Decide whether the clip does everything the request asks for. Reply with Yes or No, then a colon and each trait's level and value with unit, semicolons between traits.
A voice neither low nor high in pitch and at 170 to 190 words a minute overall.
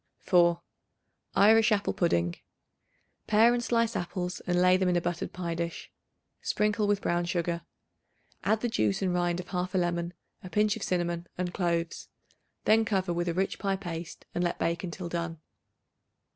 Yes: medium, 180 Hz; average, 175 wpm